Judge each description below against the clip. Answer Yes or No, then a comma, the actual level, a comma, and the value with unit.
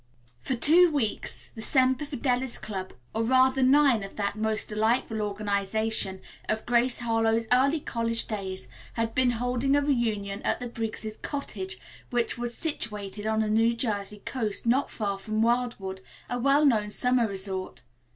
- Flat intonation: No, average, 3.2 semitones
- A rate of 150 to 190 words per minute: Yes, average, 155 wpm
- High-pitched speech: Yes, high, 225 Hz